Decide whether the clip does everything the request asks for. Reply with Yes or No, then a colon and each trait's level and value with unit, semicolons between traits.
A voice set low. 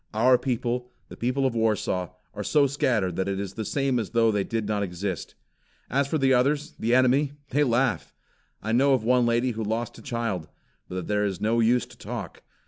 Yes: low, 115 Hz